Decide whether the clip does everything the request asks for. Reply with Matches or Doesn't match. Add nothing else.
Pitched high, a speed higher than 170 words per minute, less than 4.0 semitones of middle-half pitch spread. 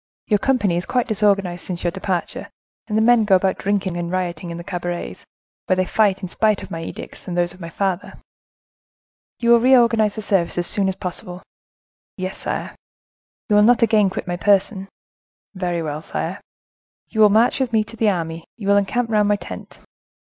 Matches